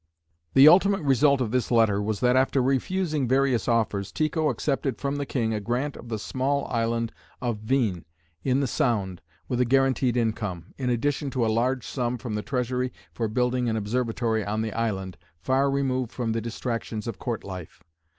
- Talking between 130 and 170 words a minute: No, average, 185 wpm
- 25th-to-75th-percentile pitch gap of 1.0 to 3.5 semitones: Yes, average, 3.2 semitones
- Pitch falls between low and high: No, low, 120 Hz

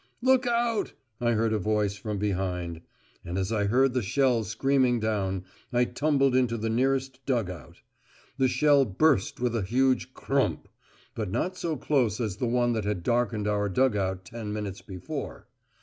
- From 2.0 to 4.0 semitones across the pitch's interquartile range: No, average, 4.4 semitones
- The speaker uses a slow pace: No, average, 175 wpm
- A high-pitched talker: No, low, 115 Hz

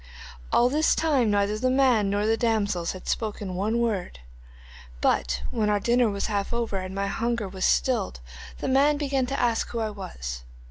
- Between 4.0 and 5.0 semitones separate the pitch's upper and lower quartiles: No, average, 3.5 semitones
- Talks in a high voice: Yes, high, 215 Hz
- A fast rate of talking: No, average, 185 wpm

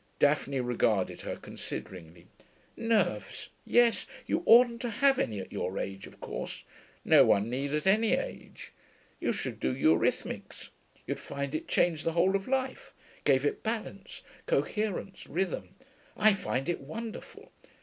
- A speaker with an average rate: Yes, average, 145 wpm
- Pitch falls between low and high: Yes, medium, 175 Hz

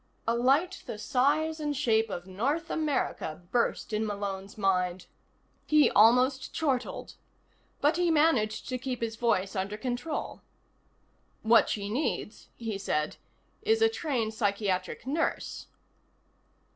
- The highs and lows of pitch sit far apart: Yes, wide, 6.4 semitones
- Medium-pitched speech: No, high, 235 Hz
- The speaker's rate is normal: No, slow, 125 wpm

